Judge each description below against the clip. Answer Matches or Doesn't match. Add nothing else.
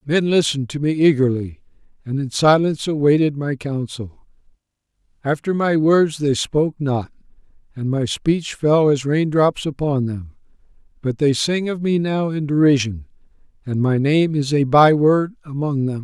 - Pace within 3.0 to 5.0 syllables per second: Matches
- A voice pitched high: Doesn't match